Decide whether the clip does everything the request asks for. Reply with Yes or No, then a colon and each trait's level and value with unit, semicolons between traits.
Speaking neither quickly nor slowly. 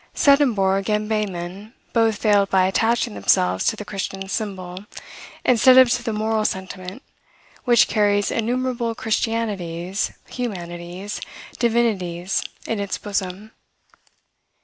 No: slow, 110 wpm